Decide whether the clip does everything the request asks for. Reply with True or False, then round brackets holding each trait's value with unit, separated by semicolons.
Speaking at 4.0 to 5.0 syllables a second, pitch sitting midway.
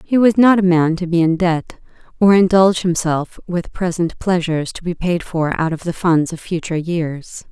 True (4.9 syllables/s; 175 Hz)